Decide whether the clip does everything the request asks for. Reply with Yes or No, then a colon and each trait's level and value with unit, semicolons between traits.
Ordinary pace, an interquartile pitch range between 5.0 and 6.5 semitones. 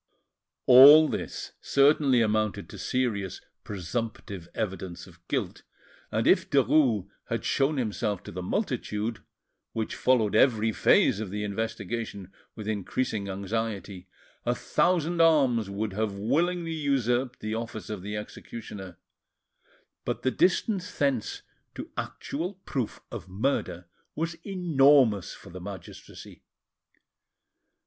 No: slow, 120 wpm; average, 5.3 semitones